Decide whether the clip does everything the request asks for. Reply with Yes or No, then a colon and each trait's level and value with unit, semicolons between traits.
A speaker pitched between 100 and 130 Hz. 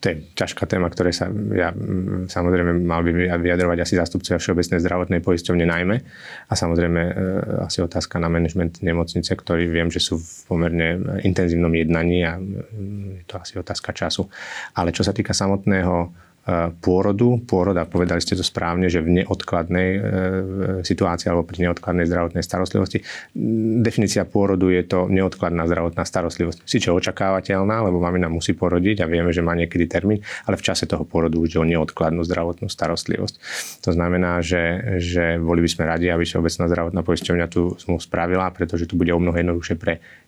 No: very low, 90 Hz